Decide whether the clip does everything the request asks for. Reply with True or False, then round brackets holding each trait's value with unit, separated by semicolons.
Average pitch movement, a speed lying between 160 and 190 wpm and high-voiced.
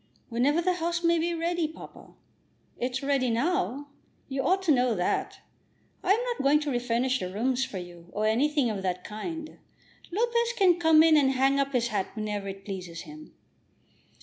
False (6.5 semitones; 180 wpm; 270 Hz)